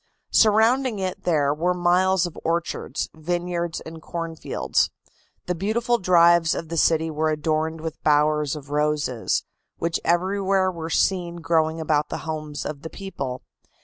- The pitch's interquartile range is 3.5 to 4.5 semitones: No, narrow, 2.6 semitones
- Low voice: No, medium, 165 Hz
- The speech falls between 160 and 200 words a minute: No, average, 150 wpm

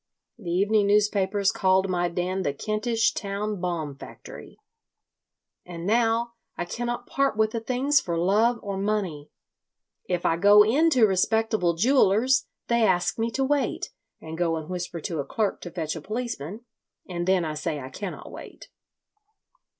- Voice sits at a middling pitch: No, high, 200 Hz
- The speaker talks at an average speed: Yes, average, 160 wpm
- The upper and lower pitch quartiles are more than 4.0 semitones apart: Yes, average, 4.4 semitones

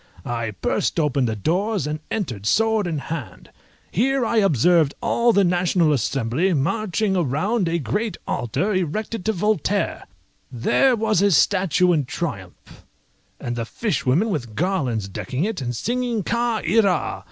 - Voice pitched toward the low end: No, medium, 175 Hz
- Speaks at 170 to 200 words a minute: No, average, 145 wpm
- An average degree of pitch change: No, wide, 7.7 semitones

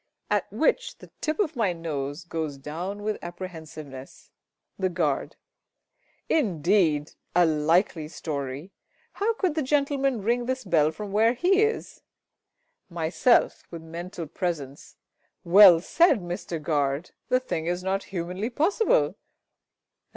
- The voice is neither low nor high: Yes, medium, 180 Hz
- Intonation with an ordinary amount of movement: No, wide, 7.1 semitones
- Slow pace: Yes, slow, 125 wpm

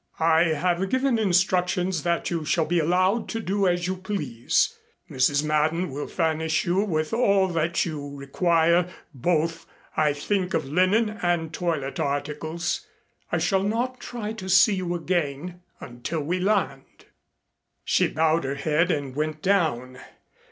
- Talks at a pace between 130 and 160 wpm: Yes, average, 145 wpm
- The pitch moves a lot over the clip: No, average, 3.6 semitones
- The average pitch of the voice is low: No, medium, 170 Hz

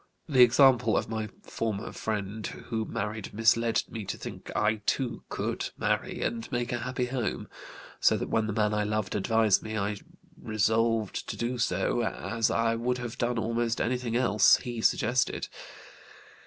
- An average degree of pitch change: No, narrow, 2.0 semitones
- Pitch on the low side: Yes, low, 115 Hz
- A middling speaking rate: Yes, average, 165 wpm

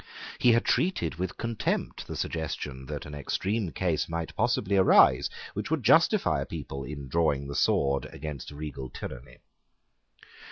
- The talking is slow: No, average, 150 wpm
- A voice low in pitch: Yes, very low, 75 Hz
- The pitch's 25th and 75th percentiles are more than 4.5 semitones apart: Yes, average, 5.1 semitones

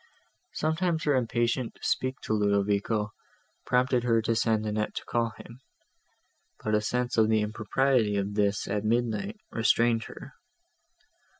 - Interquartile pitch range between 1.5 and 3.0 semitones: Yes, average, 2.7 semitones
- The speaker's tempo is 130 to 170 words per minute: Yes, average, 140 wpm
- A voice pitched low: Yes, low, 115 Hz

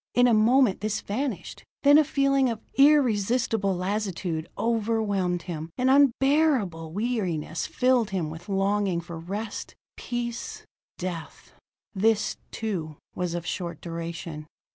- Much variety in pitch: Yes, wide, 5.8 semitones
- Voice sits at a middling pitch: No, high, 205 Hz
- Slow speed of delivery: Yes, slow, 120 wpm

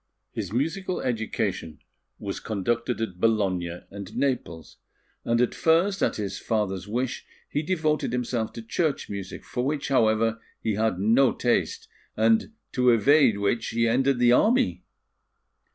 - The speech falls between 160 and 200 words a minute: No, average, 140 wpm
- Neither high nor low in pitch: No, low, 115 Hz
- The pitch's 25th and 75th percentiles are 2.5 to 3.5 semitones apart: No, average, 4.1 semitones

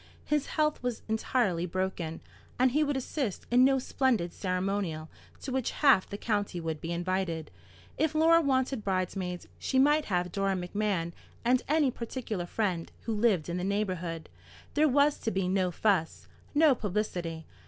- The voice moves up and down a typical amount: No, wide, 6.5 semitones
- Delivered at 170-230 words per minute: No, average, 160 wpm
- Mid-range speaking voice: No, high, 205 Hz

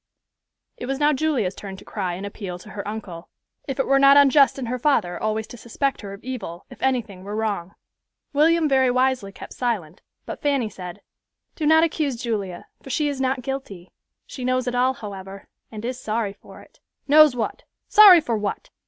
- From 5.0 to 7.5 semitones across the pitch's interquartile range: Yes, average, 5.3 semitones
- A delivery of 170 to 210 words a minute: Yes, average, 195 wpm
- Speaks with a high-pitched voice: Yes, high, 245 Hz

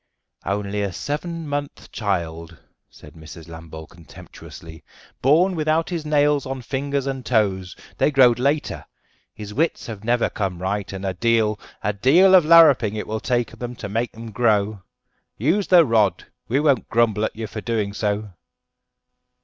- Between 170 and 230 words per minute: No, average, 155 wpm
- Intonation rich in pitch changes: Yes, wide, 6.0 semitones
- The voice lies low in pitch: Yes, low, 115 Hz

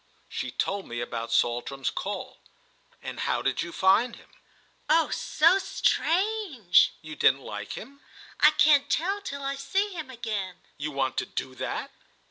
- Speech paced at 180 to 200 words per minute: No, average, 155 wpm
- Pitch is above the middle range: Yes, high, 235 Hz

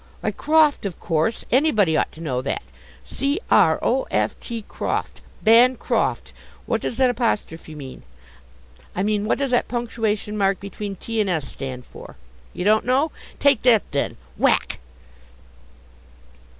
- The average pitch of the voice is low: No, high, 215 Hz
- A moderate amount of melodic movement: No, wide, 5.9 semitones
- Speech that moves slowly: No, average, 150 wpm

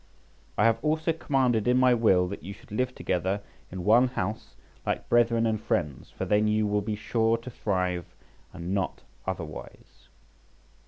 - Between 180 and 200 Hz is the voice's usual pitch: No, low, 110 Hz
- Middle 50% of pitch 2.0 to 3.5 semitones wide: No, average, 4.0 semitones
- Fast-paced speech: No, average, 165 wpm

